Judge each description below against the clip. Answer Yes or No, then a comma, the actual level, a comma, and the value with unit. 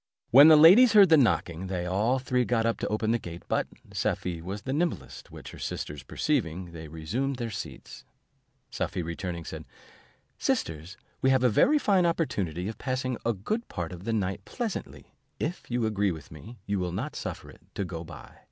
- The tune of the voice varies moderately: No, wide, 7.0 semitones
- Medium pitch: No, low, 110 Hz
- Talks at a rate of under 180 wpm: No, average, 200 wpm